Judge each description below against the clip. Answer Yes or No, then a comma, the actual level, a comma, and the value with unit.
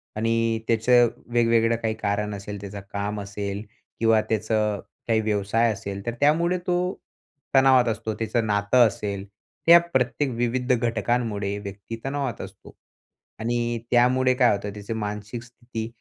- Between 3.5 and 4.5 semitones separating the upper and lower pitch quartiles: No, average, 2.8 semitones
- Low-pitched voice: Yes, low, 115 Hz